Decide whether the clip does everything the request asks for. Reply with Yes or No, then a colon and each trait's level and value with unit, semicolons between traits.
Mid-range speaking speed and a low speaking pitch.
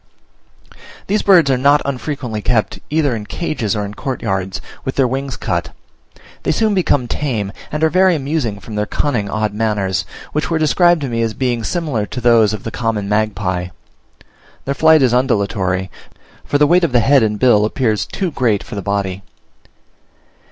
Yes: average, 180 wpm; low, 120 Hz